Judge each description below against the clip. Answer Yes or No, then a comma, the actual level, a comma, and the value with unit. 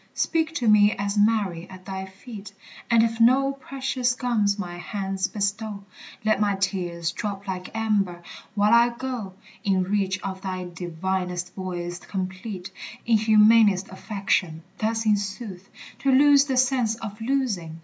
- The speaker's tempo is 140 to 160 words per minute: Yes, average, 150 wpm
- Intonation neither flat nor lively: Yes, average, 3.3 semitones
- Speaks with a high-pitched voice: Yes, high, 205 Hz